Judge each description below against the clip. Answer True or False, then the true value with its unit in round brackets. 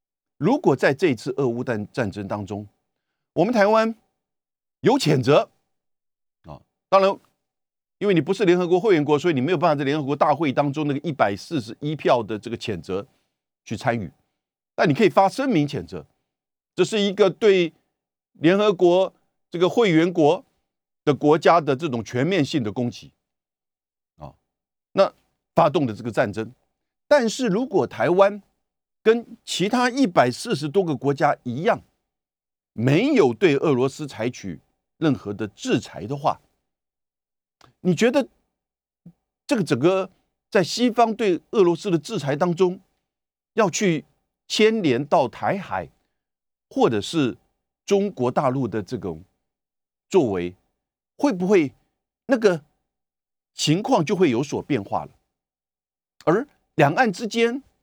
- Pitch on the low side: False (165 Hz)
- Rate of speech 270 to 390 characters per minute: False (205 characters per minute)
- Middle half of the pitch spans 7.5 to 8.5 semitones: True (7.9 semitones)